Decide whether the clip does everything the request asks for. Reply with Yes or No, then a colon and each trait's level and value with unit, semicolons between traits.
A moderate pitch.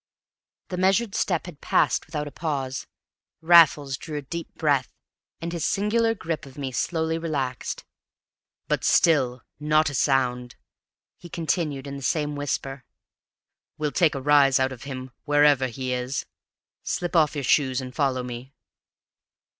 Yes: medium, 145 Hz